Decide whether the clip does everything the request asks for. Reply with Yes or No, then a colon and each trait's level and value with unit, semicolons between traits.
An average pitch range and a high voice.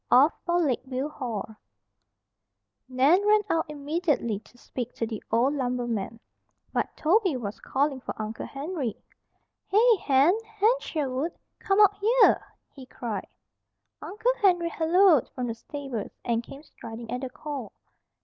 No: wide, 6.4 semitones; very high, 280 Hz